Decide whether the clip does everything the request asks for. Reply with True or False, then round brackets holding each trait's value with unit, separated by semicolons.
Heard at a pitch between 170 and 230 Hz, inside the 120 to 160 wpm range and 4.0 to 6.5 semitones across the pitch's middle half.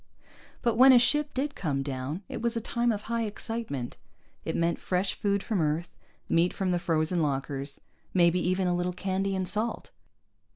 False (185 Hz; 180 wpm; 5.4 semitones)